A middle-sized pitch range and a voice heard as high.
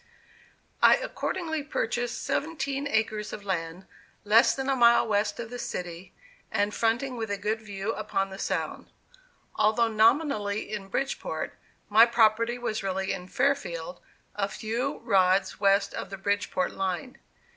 Yes: average, 3.5 semitones; high, 215 Hz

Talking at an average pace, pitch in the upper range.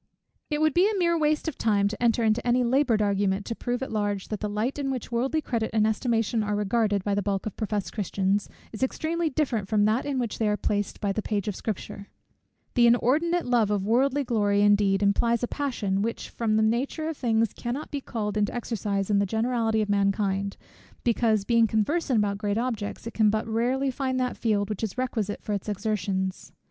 No: fast, 210 wpm; high, 220 Hz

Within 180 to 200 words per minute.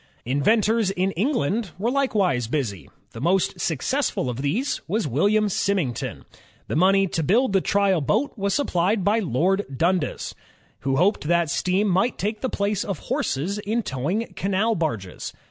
No: average, 155 wpm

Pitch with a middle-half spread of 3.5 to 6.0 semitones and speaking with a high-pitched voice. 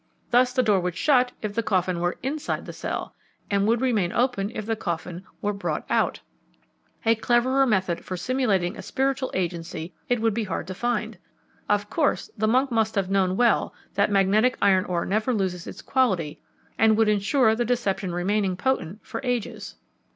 Yes: average, 4.5 semitones; high, 210 Hz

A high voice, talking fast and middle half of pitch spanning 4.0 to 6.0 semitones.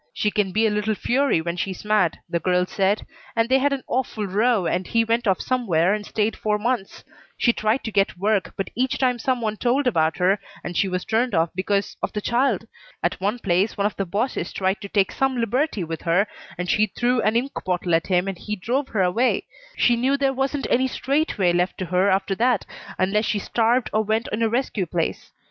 Yes: high, 210 Hz; fast, 230 wpm; average, 4.4 semitones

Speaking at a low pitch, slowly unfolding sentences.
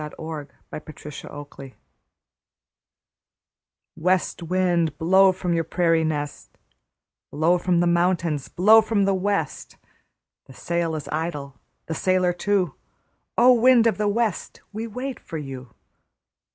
No: medium, 175 Hz; slow, 130 wpm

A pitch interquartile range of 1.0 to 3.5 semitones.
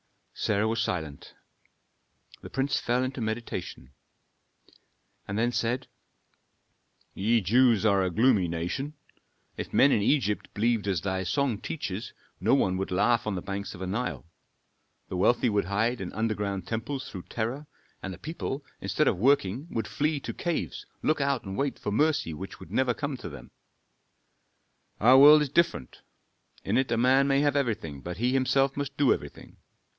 No: wide, 5.5 semitones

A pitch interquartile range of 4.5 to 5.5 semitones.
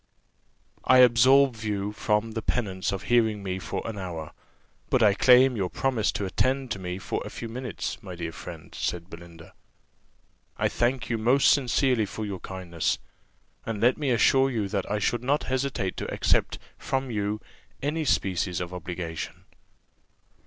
Yes: average, 5.1 semitones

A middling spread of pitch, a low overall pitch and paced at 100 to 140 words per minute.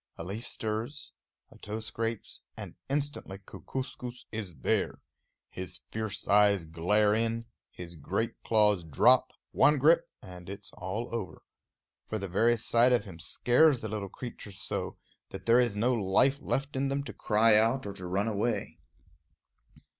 No: average, 3.6 semitones; low, 110 Hz; average, 155 wpm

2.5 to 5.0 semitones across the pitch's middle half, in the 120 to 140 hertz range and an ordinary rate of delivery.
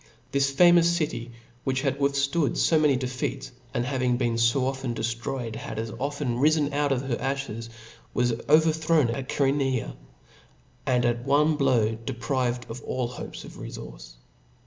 Yes: average, 3.0 semitones; low, 135 Hz; average, 160 wpm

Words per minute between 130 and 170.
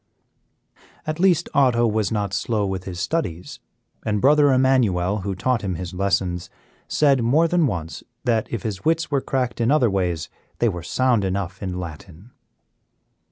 Yes: average, 160 wpm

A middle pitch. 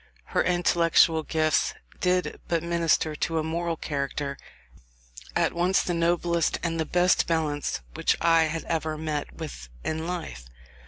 Yes: medium, 165 Hz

